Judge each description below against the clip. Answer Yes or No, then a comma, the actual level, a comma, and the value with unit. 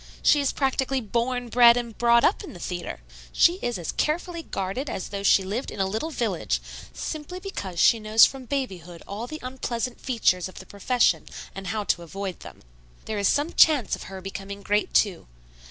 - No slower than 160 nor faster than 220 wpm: Yes, average, 195 wpm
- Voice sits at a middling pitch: No, high, 230 Hz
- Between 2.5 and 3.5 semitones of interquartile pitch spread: No, average, 5.2 semitones